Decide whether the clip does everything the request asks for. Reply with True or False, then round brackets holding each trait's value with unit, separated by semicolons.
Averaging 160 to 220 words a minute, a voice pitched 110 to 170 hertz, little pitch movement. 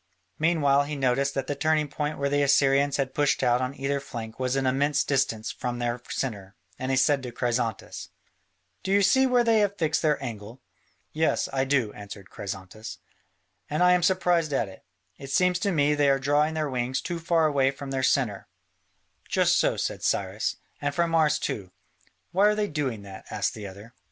False (195 wpm; 140 Hz; 4.0 semitones)